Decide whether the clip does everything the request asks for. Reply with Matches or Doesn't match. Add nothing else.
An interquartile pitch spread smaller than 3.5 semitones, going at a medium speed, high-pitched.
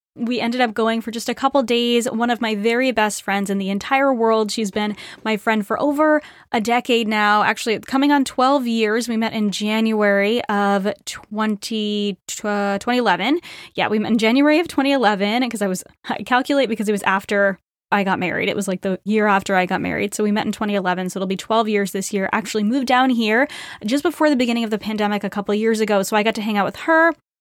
Doesn't match